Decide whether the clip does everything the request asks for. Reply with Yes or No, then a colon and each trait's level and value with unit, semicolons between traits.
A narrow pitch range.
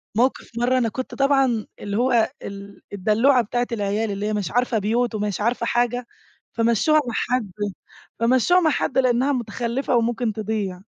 No: average, 3.0 semitones